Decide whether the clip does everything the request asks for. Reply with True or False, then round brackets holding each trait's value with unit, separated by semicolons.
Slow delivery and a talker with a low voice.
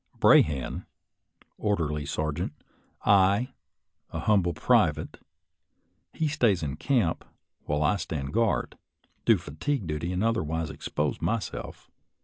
True (110 wpm; 85 Hz)